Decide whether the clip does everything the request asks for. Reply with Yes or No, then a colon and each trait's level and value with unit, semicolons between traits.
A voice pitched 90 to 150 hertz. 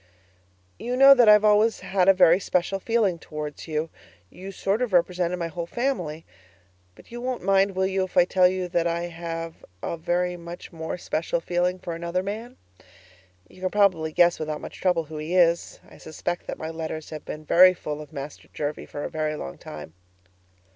No: medium, 175 Hz